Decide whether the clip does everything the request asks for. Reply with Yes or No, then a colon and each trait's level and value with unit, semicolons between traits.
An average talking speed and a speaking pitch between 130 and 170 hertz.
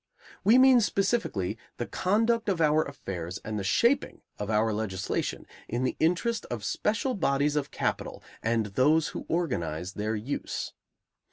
Yes: average, 150 wpm; medium, 140 Hz